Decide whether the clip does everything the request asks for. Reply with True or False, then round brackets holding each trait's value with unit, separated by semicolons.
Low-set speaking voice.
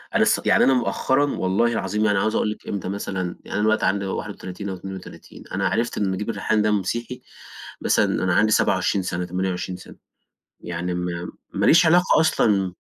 True (100 Hz)